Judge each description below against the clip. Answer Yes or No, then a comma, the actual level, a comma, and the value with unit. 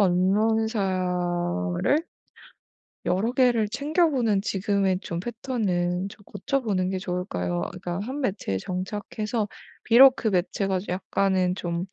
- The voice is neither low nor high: No, high, 195 Hz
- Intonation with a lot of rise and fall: No, average, 3.7 semitones